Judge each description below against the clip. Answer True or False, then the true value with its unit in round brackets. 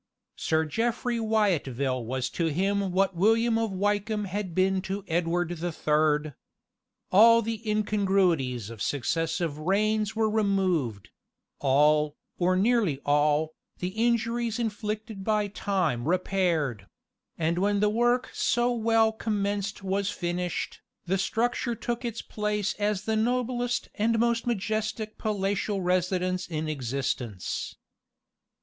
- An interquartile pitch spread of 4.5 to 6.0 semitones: True (5.0 semitones)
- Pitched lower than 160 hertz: False (195 Hz)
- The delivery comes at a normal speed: False (120 wpm)